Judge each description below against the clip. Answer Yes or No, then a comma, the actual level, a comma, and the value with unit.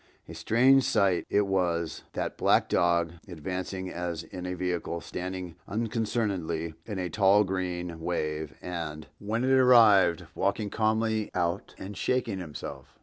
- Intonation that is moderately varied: Yes, average, 3.6 semitones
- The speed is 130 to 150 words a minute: Yes, slow, 135 wpm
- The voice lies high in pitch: No, very low, 95 Hz